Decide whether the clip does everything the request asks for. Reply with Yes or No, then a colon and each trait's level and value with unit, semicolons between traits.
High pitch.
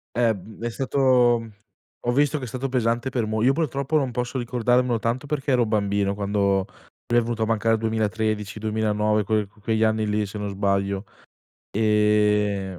No: low, 110 Hz